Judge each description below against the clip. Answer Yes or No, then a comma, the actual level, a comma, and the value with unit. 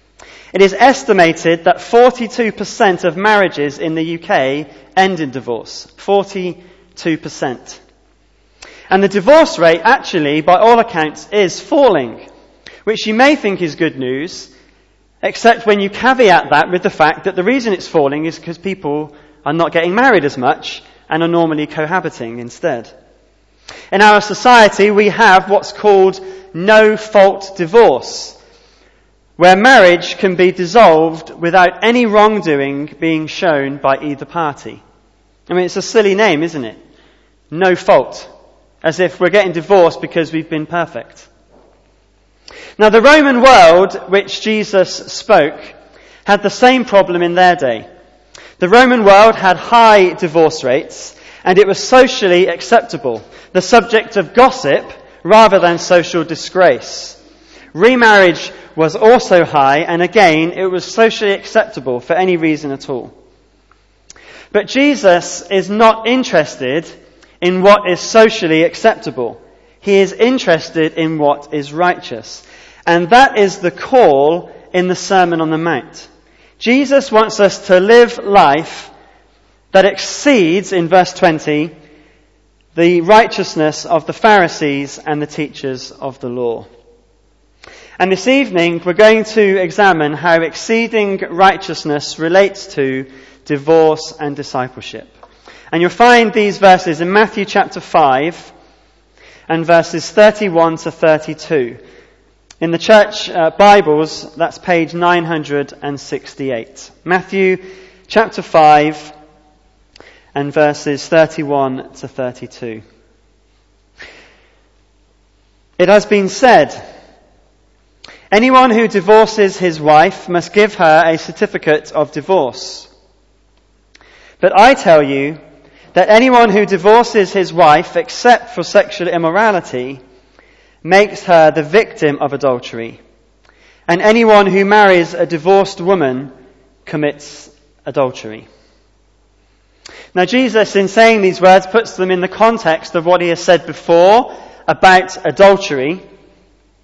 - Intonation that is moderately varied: Yes, average, 4.9 semitones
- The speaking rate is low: Yes, slow, 125 wpm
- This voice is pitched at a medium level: Yes, medium, 180 Hz